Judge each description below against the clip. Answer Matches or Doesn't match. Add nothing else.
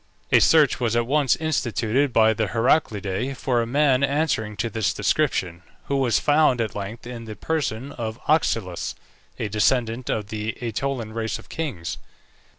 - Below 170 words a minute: Matches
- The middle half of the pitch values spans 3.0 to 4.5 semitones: Matches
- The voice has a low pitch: Matches